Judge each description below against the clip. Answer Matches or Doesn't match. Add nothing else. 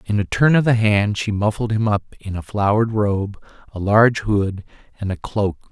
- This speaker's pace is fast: Matches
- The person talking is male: Matches